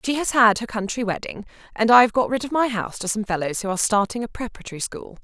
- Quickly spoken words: Yes, fast, 250 wpm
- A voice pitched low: No, high, 225 Hz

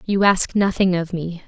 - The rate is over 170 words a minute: Yes, fast, 205 wpm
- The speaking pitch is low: No, medium, 185 Hz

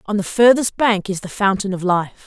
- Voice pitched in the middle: No, high, 200 Hz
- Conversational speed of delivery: No, fast, 240 wpm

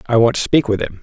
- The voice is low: Yes, low, 120 Hz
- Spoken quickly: Yes, fast, 350 wpm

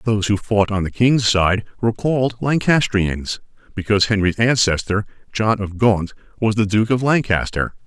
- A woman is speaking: No, male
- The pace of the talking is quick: No, average, 160 wpm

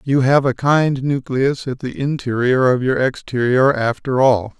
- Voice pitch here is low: Yes, low, 130 Hz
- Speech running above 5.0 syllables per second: No, 4.3 syllables/s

